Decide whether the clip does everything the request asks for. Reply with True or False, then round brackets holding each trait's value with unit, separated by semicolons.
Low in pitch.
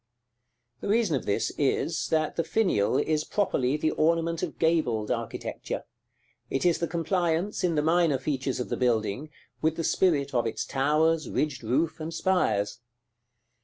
False (155 Hz)